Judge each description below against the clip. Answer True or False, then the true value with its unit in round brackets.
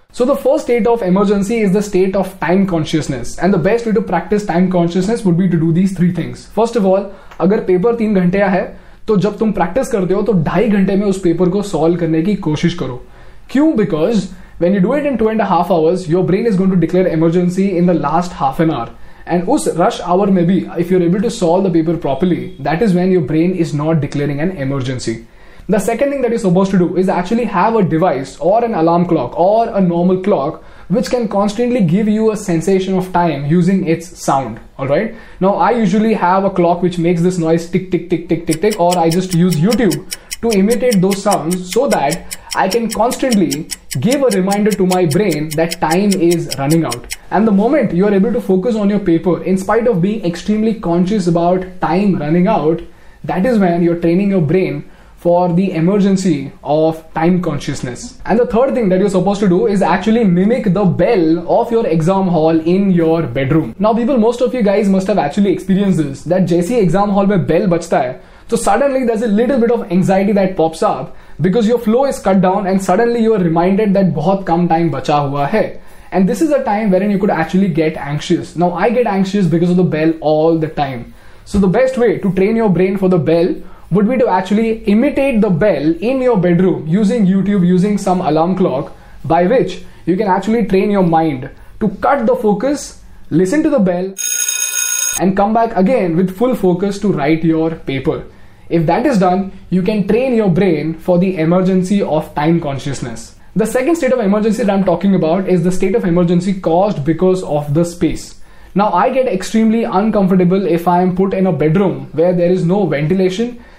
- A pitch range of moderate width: True (3.7 semitones)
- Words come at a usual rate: False (215 wpm)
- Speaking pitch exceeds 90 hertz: True (185 Hz)